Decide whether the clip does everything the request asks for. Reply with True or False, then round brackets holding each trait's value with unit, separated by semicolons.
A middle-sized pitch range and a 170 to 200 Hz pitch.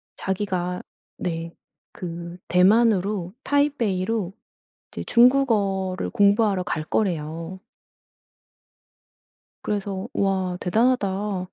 True (3.0 semitones; 190 Hz)